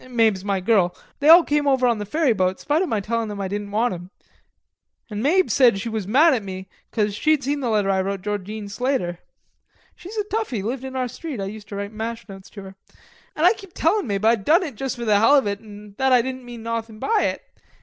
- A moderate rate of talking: No, fast, 250 wpm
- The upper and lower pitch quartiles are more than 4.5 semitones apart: Yes, average, 5.1 semitones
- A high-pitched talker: Yes, high, 225 Hz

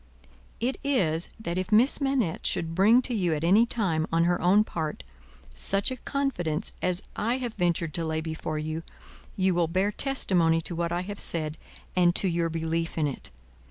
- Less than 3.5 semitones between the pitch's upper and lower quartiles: No, average, 4.4 semitones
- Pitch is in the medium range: Yes, medium, 175 Hz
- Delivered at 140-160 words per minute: No, average, 190 wpm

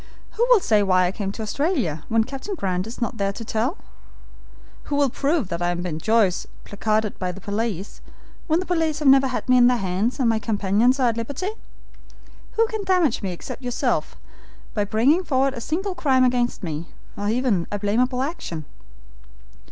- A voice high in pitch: Yes, high, 230 Hz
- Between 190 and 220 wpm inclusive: Yes, average, 195 wpm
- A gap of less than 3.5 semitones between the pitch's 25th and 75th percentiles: No, wide, 5.5 semitones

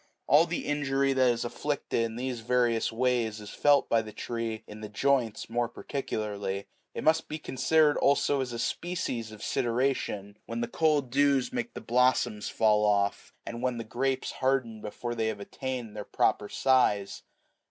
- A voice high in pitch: No, low, 120 Hz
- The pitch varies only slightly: No, average, 3.6 semitones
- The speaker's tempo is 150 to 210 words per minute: Yes, average, 175 wpm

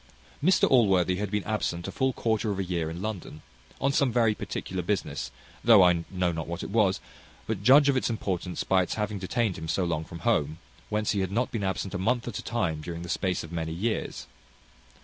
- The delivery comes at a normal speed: No, fast, 225 wpm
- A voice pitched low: Yes, very low, 95 Hz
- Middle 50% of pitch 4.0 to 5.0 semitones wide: Yes, average, 4.4 semitones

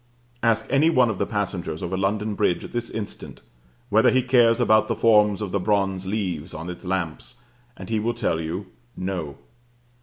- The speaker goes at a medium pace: Yes, average, 185 wpm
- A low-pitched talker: Yes, low, 105 Hz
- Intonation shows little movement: No, average, 3.8 semitones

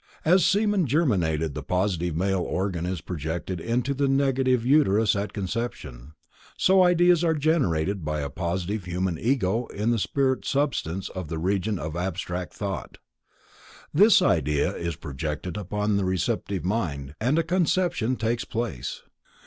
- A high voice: No, low, 100 Hz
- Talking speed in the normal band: Yes, average, 150 wpm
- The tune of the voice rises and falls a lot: Yes, wide, 7.7 semitones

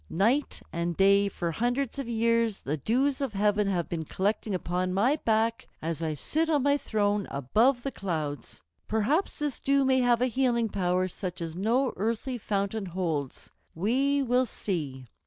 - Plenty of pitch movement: Yes, wide, 5.8 semitones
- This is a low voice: No, high, 210 Hz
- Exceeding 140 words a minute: Yes, average, 170 wpm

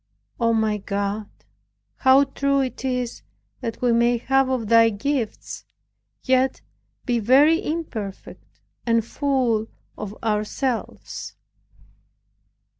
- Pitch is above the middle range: Yes, high, 240 Hz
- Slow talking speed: Yes, slow, 110 wpm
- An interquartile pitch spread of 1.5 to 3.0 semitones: No, average, 3.4 semitones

